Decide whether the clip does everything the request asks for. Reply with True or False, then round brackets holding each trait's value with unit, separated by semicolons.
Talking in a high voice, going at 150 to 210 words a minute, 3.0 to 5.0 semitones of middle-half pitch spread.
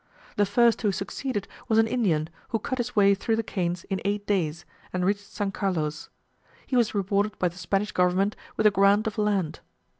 False (200 Hz; 200 wpm; 2.6 semitones)